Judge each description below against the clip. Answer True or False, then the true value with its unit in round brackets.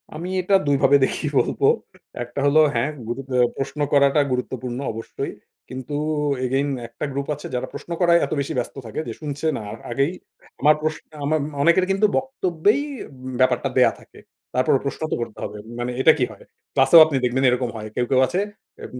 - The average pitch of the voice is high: False (140 Hz)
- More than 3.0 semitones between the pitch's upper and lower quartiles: True (3.8 semitones)